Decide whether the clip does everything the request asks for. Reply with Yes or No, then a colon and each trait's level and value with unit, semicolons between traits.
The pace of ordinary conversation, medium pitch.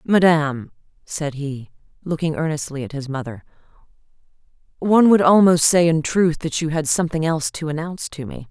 Yes: average, 160 wpm; medium, 155 Hz